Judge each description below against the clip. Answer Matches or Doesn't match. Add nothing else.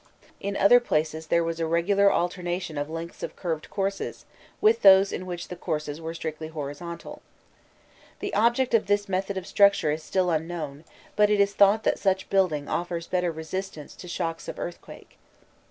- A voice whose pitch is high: Doesn't match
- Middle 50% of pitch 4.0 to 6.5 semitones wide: Doesn't match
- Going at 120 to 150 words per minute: Doesn't match